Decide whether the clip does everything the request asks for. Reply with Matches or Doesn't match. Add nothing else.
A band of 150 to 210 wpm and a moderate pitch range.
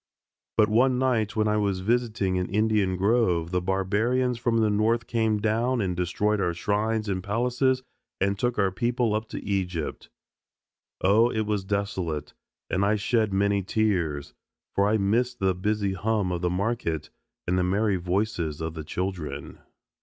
Matches